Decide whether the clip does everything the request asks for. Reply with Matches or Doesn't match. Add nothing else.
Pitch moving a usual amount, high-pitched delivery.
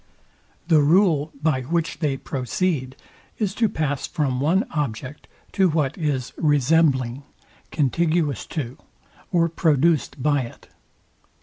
Doesn't match